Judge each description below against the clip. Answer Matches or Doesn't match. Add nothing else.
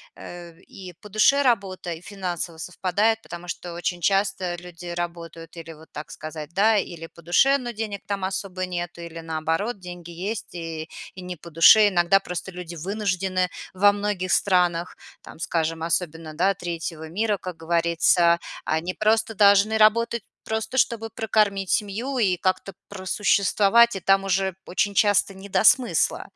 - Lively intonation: Doesn't match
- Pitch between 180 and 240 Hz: Matches